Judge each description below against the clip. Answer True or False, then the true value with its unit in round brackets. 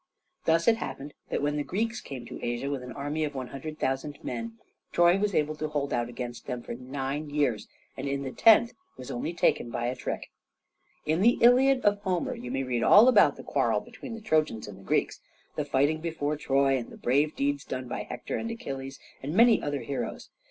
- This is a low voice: False (145 Hz)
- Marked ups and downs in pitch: False (4.8 semitones)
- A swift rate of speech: True (210 wpm)